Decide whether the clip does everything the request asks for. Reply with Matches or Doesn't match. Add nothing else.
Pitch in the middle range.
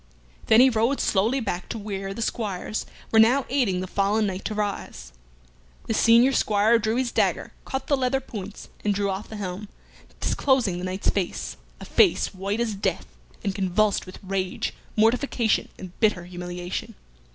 Doesn't match